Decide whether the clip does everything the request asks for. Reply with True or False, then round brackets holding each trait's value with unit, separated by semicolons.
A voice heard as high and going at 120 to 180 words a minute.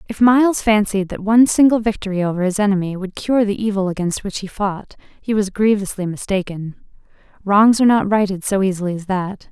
False (200 Hz; 190 wpm)